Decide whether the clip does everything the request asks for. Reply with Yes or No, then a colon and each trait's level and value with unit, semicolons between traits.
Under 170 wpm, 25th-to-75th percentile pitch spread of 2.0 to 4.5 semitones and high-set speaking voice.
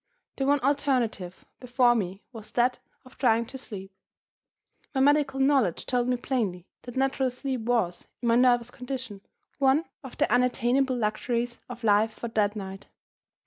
Yes: average, 155 wpm; average, 3.3 semitones; high, 245 Hz